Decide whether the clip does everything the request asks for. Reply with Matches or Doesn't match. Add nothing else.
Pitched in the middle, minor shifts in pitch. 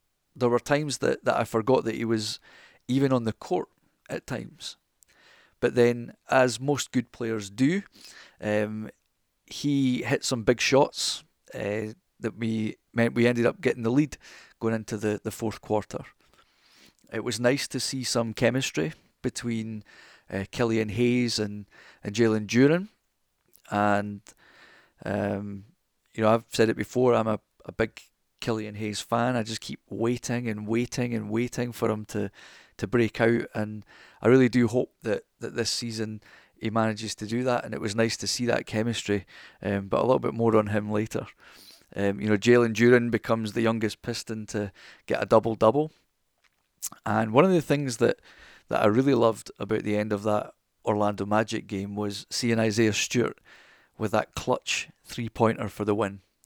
Doesn't match